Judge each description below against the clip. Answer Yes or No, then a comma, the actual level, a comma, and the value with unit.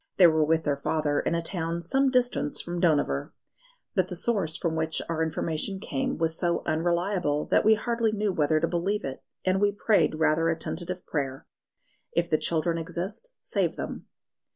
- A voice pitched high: No, medium, 170 Hz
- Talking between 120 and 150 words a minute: No, average, 180 wpm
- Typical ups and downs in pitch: Yes, average, 3.5 semitones